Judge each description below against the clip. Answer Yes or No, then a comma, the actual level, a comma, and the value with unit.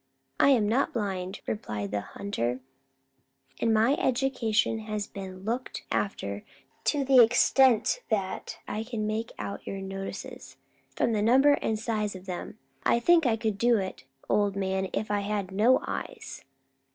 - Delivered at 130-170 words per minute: Yes, average, 155 wpm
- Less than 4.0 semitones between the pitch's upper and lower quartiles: Yes, average, 3.5 semitones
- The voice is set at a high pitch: Yes, high, 215 Hz